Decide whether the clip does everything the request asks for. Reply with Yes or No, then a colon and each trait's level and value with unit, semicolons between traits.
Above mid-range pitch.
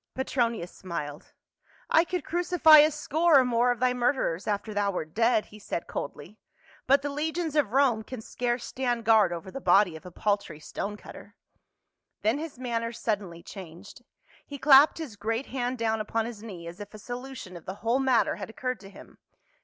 Yes: high, 230 Hz